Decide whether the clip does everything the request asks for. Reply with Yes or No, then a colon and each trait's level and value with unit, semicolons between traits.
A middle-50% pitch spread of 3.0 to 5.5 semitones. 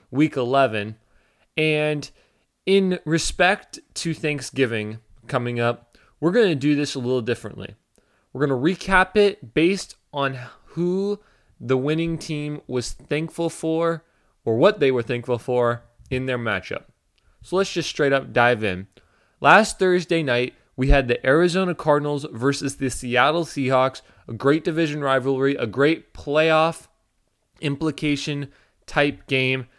Yes: average, 4.4 semitones